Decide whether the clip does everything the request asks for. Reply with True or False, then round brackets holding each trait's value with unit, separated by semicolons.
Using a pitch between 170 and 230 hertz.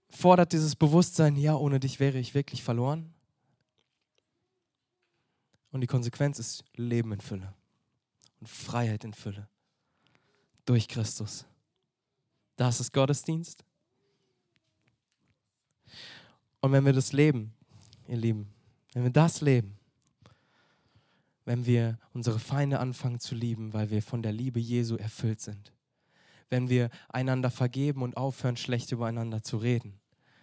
False (125 Hz)